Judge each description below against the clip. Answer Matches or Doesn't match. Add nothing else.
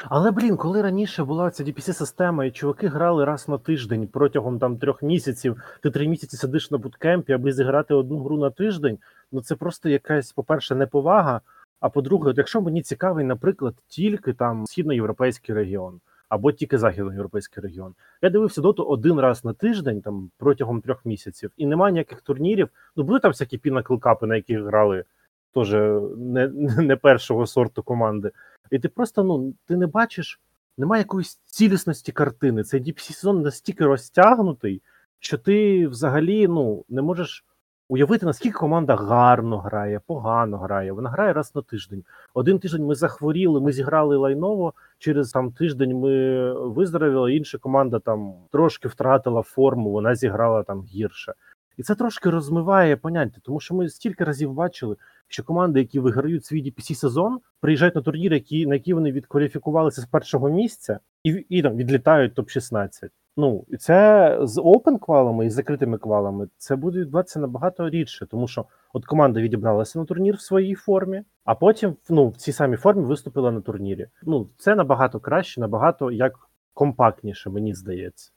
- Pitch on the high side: Doesn't match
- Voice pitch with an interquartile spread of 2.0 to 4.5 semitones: Doesn't match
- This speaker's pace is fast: Matches